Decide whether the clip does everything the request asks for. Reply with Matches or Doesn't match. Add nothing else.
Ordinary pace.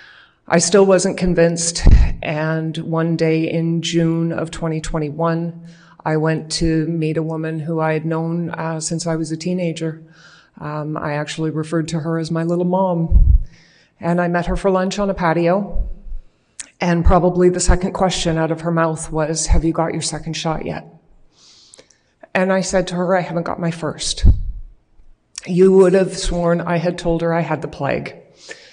Matches